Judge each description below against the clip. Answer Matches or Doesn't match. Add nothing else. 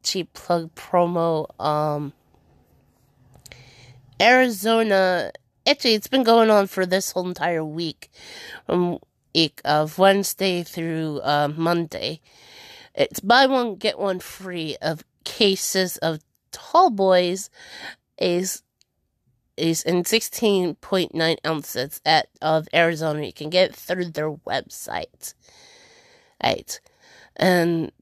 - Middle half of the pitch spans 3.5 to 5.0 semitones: Matches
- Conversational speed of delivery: Doesn't match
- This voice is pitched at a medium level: Matches